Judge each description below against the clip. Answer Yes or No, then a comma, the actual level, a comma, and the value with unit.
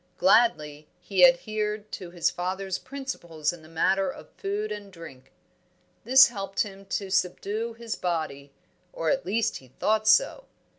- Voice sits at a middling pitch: No, high, 195 Hz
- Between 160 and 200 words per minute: No, average, 150 wpm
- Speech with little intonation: No, average, 3.9 semitones